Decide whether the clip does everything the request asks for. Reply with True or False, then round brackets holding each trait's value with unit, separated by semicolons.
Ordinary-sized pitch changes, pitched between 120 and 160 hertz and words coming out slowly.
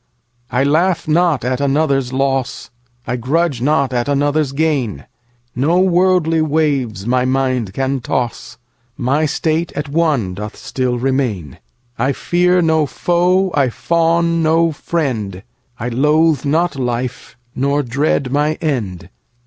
True (4.5 semitones; 140 Hz; 115 wpm)